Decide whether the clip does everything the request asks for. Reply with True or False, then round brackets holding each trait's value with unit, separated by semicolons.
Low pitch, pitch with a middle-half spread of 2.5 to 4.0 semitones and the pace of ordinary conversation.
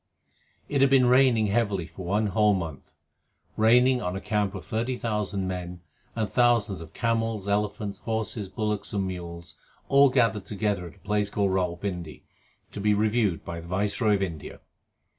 True (105 Hz; 3.2 semitones; 170 wpm)